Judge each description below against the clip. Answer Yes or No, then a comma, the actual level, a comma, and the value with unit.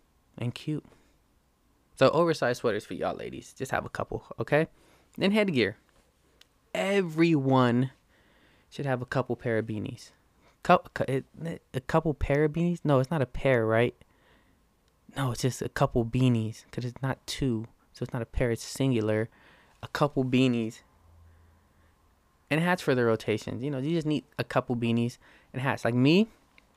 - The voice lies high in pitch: No, low, 125 Hz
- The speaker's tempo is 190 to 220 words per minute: No, average, 160 wpm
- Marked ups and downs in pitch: No, average, 4.1 semitones